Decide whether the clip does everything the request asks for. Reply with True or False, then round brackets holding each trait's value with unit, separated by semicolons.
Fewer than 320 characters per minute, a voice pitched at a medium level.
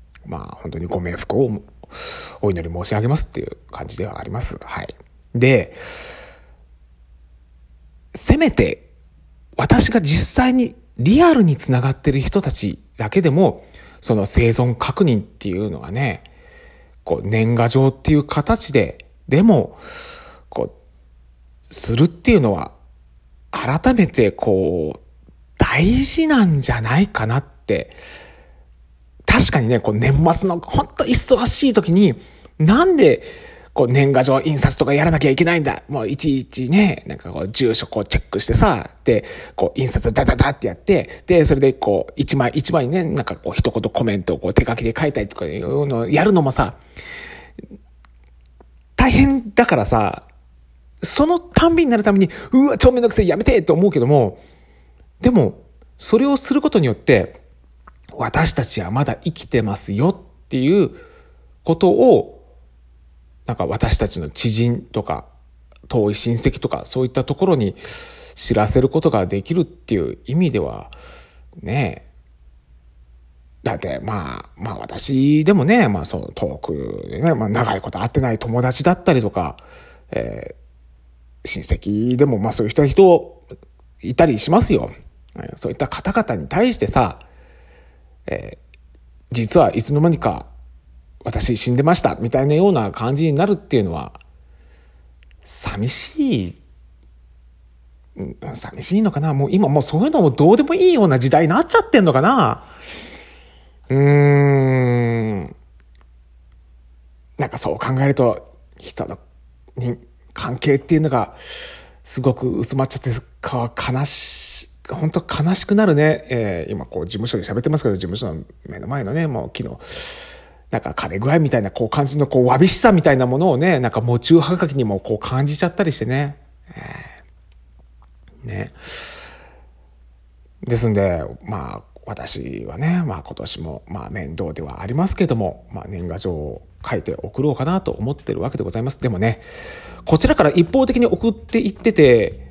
False (290 characters per minute; 120 Hz)